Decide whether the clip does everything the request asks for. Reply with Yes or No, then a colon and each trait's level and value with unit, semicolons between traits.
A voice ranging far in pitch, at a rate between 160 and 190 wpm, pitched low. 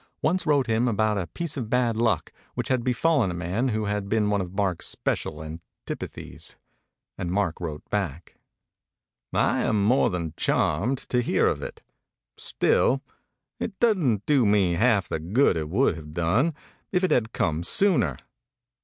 Yes: wide, 6.4 semitones; average, 165 wpm; low, 105 Hz